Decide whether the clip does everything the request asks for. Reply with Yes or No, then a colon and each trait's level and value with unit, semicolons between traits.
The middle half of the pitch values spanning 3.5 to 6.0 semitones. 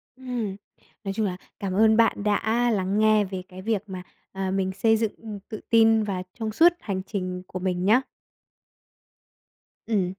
No: average, 2.9 semitones